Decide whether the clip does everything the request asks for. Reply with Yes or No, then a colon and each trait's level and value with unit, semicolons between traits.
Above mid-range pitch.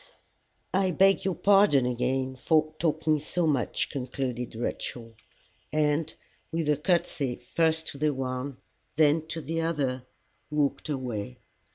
No: medium, 150 Hz